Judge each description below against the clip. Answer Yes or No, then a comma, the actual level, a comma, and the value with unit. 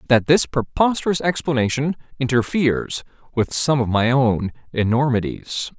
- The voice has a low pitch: Yes, low, 125 Hz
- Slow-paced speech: Yes, slow, 115 wpm